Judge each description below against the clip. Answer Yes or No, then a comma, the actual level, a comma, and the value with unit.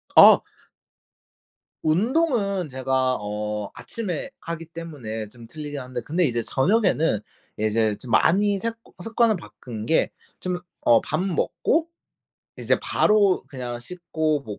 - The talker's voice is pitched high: No, medium, 155 Hz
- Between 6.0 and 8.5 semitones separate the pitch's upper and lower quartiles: Yes, wide, 7.9 semitones